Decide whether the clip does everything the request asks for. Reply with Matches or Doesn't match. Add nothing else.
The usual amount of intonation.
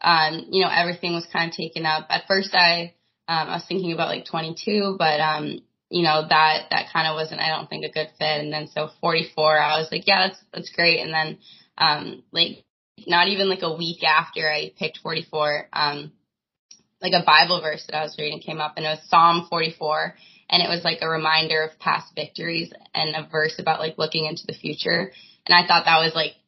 Doesn't match